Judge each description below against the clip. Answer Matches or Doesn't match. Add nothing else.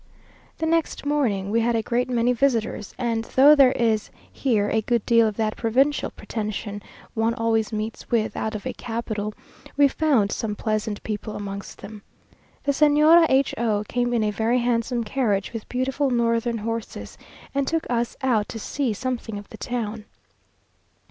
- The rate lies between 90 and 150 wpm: Doesn't match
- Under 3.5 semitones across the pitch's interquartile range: Matches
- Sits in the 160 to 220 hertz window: Doesn't match